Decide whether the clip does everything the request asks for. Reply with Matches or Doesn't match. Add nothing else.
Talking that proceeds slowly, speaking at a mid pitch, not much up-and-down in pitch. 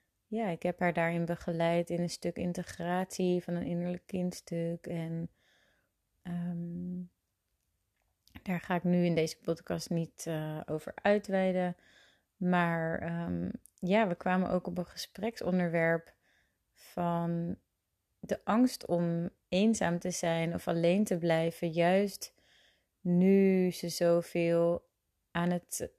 Matches